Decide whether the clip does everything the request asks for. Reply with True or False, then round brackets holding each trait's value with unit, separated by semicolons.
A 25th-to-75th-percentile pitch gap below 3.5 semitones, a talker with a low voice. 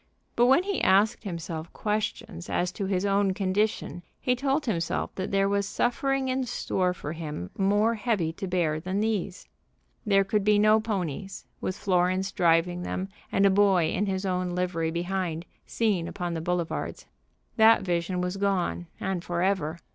False (2.9 semitones; 190 Hz)